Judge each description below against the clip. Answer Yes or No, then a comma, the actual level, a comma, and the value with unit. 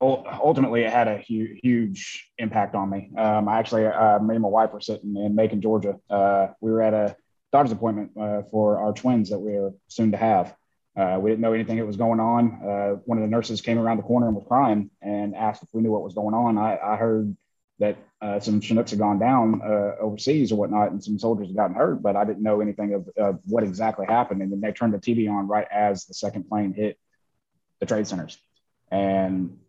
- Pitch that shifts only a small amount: Yes, narrow, 1.7 semitones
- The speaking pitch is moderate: No, low, 105 Hz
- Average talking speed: No, fast, 235 wpm